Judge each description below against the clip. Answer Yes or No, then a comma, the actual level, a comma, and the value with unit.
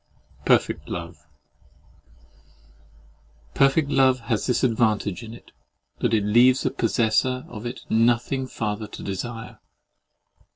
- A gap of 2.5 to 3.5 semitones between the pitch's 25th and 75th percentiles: Yes, average, 3.2 semitones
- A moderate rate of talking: No, slow, 115 wpm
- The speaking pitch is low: Yes, low, 115 Hz